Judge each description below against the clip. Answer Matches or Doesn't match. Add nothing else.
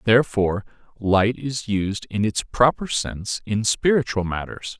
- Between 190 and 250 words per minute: Doesn't match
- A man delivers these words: Matches